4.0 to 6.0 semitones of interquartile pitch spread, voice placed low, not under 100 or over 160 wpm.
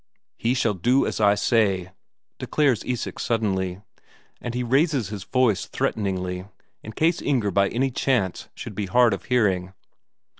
Yes: average, 4.5 semitones; low, 110 Hz; average, 150 wpm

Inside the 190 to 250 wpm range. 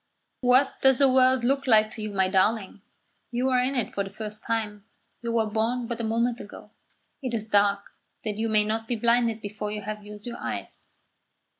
Yes: fast, 205 wpm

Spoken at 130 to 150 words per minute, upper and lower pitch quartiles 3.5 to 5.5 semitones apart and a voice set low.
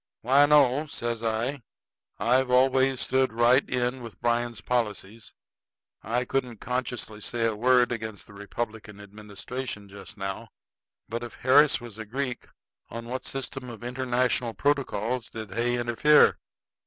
No: average, 140 wpm; narrow, 2.5 semitones; low, 120 Hz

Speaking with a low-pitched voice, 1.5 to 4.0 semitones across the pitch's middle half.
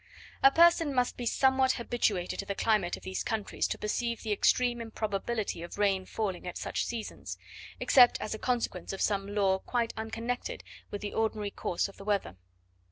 No: high, 220 Hz; average, 3.4 semitones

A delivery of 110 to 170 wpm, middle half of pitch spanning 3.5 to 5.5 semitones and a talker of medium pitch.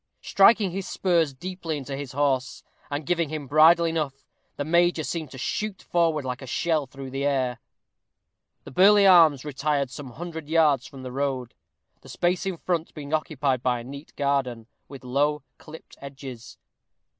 Yes: average, 165 wpm; average, 3.8 semitones; medium, 145 Hz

